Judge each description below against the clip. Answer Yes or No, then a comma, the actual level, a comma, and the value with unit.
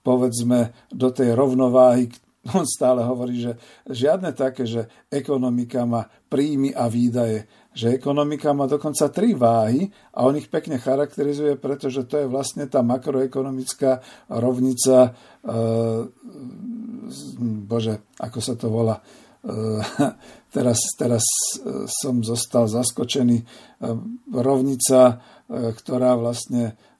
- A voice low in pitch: Yes, low, 125 Hz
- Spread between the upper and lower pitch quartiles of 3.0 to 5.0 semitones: No, narrow, 2.5 semitones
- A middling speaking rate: No, slow, 105 wpm